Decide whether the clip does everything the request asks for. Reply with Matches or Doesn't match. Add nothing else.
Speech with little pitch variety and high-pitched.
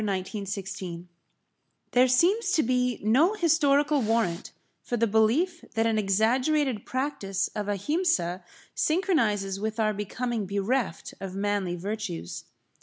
Doesn't match